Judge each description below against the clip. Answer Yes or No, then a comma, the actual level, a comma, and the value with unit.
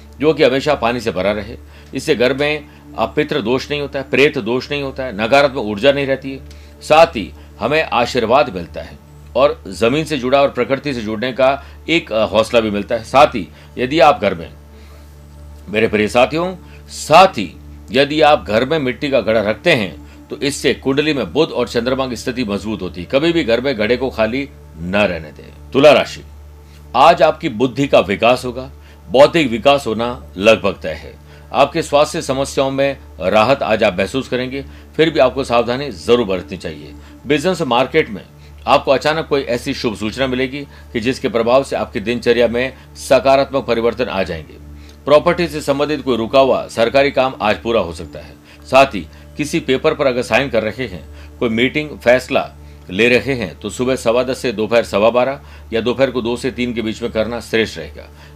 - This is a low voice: Yes, low, 120 Hz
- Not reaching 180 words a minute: No, fast, 190 wpm